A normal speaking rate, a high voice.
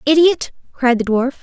Yes: average, 170 wpm; very high, 275 Hz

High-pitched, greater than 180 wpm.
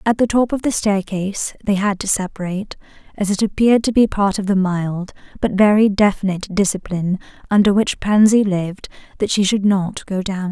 Yes: high, 200 Hz; average, 190 wpm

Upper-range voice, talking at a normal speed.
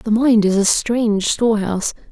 Yes: high, 215 Hz; average, 170 wpm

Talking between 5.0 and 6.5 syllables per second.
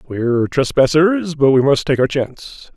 No: 4.7 syllables/s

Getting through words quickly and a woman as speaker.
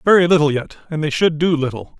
No: fast, 240 wpm; male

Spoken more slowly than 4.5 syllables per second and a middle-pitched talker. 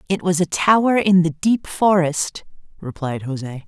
Yes: 4.1 syllables/s; medium, 170 Hz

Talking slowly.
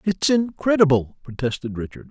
Yes: slow, 115 wpm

